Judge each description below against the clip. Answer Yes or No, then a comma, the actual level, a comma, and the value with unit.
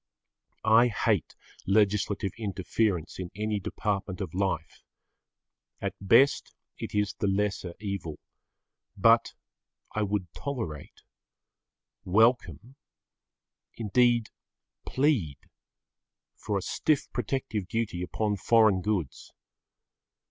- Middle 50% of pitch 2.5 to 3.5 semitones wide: Yes, average, 3.2 semitones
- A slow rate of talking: Yes, slow, 90 wpm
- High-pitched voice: No, low, 105 Hz